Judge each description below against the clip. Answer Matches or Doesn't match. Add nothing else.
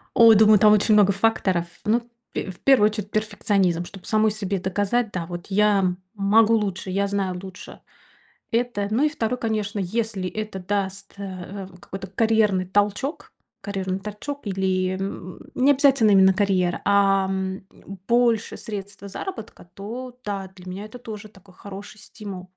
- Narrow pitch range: Matches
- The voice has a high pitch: Matches